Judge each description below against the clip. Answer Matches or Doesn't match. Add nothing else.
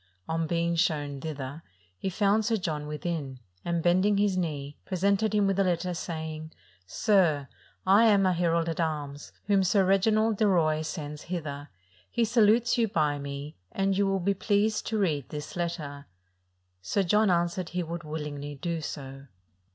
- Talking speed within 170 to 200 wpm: Matches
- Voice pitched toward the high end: Doesn't match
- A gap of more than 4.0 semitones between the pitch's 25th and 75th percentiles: Matches